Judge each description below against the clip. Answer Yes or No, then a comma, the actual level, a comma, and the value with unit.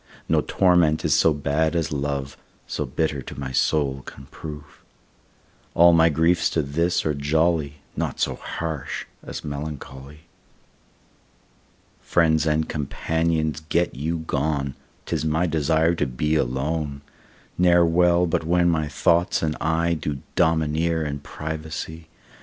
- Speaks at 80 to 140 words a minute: Yes, slow, 135 wpm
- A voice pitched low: Yes, very low, 80 Hz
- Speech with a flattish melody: Yes, narrow, 2.3 semitones